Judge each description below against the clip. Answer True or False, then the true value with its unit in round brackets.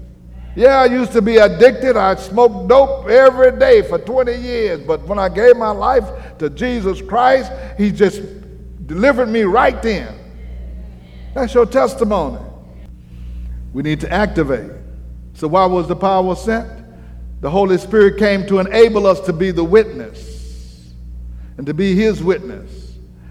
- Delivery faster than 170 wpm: False (150 wpm)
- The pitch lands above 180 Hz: True (190 Hz)